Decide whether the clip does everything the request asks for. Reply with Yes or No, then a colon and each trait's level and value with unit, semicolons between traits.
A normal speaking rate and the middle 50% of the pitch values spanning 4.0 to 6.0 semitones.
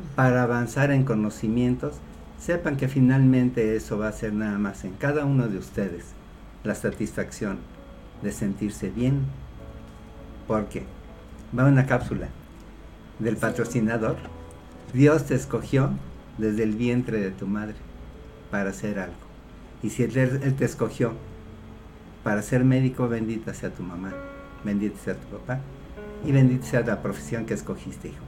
Yes: average, 140 wpm; average, 4.5 semitones